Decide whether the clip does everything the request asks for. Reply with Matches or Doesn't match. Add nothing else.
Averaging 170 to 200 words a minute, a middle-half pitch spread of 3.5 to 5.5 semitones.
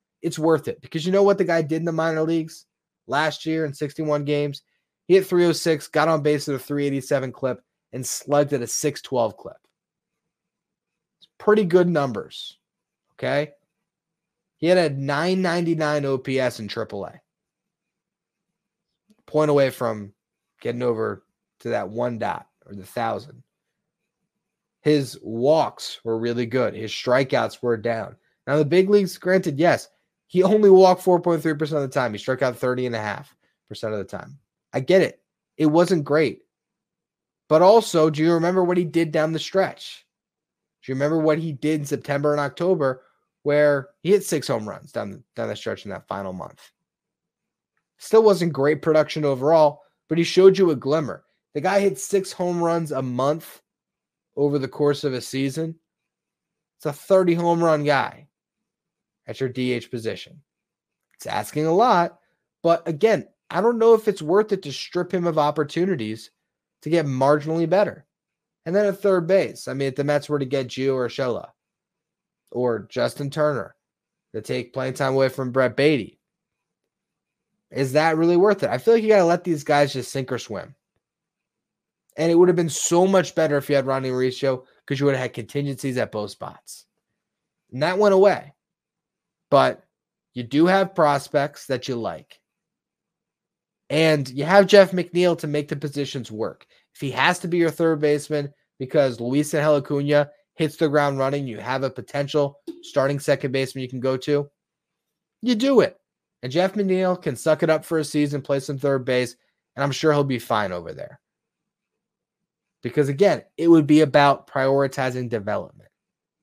Matches